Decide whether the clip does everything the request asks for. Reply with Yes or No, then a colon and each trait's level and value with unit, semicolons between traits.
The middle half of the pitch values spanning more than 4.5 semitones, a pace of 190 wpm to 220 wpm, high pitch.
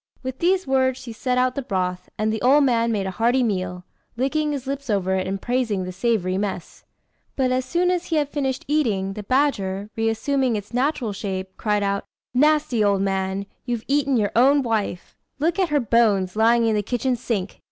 Yes: average, 5.1 semitones; average, 200 wpm; high, 235 Hz